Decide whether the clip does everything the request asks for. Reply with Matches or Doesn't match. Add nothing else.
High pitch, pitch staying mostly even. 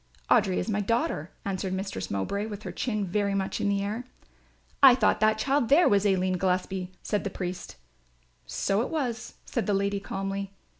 Matches